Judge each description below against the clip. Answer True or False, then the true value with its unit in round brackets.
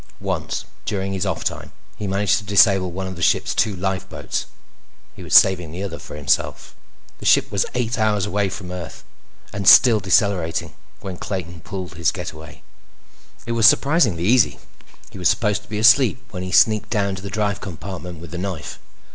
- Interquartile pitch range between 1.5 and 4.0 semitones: True (2.6 semitones)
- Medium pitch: False (95 Hz)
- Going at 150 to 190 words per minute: True (185 wpm)